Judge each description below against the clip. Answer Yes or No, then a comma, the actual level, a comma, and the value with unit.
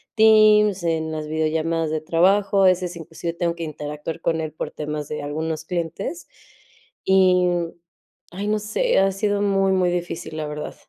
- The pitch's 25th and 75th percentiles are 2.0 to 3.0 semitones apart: No, average, 3.6 semitones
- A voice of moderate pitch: Yes, medium, 170 Hz